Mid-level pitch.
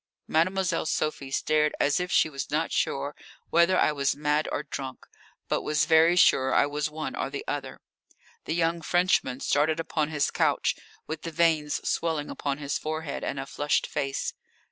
Yes: medium, 150 Hz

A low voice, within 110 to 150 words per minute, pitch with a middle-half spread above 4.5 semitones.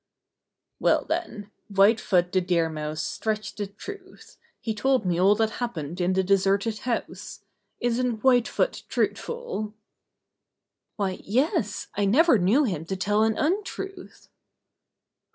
No: high, 215 Hz; average, 140 wpm; average, 5.0 semitones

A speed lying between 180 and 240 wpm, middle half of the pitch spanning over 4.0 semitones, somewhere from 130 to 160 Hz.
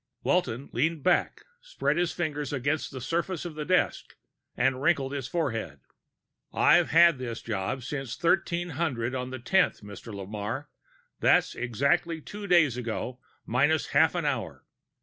No: average, 145 wpm; wide, 5.4 semitones; medium, 140 Hz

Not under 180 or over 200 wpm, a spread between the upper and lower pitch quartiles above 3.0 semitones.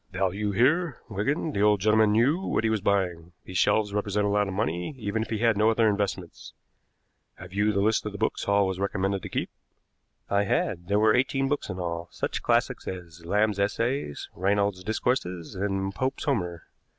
No: average, 195 wpm; average, 2.7 semitones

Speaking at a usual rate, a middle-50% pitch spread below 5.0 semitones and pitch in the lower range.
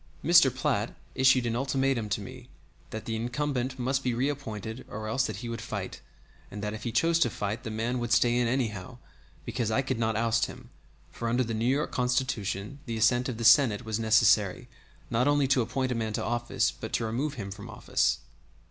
No: fast, 210 wpm; average, 2.8 semitones; low, 120 Hz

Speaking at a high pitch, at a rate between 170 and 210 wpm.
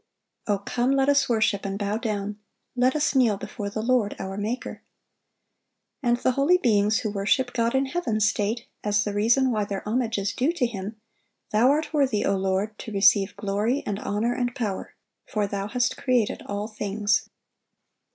Yes: high, 220 Hz; average, 180 wpm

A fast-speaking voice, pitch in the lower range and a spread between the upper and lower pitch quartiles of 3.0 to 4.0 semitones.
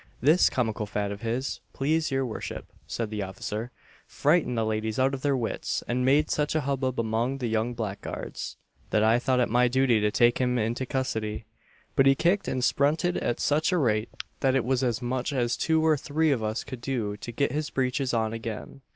Yes: fast, 210 wpm; low, 125 Hz; average, 3.5 semitones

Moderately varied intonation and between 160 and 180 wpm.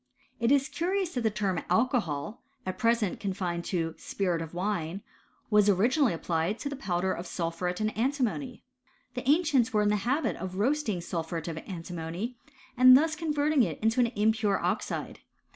No: wide, 6.2 semitones; average, 170 wpm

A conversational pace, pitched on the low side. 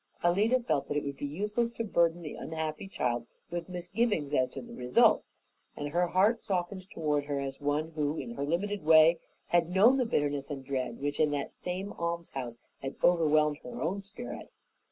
No: average, 190 wpm; medium, 165 Hz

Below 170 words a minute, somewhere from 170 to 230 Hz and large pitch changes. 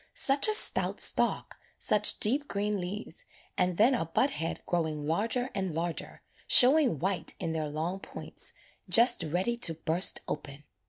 Yes: average, 155 wpm; high, 190 Hz; wide, 6.6 semitones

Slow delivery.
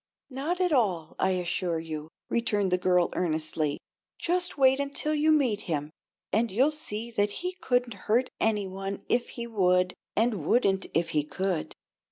No: average, 165 wpm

